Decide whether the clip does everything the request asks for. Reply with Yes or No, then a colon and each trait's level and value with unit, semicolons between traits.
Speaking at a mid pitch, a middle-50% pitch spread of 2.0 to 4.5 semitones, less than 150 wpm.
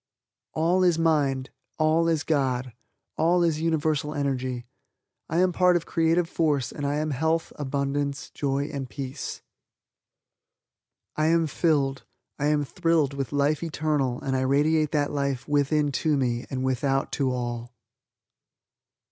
Yes: medium, 145 Hz; average, 2.9 semitones; average, 140 wpm